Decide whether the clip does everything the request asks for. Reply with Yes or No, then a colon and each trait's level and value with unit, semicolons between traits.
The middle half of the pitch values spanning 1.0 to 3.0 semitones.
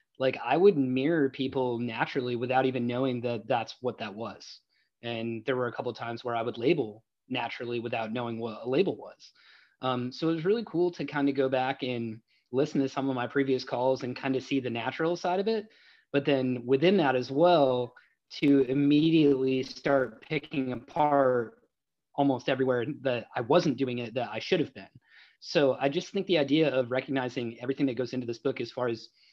Yes: narrow, 2.4 semitones